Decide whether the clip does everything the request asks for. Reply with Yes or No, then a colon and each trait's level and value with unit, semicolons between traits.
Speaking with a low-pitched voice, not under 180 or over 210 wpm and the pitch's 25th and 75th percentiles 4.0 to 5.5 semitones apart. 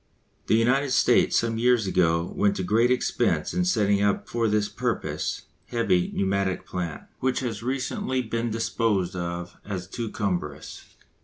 No: low, 105 Hz; average, 150 wpm; average, 4.4 semitones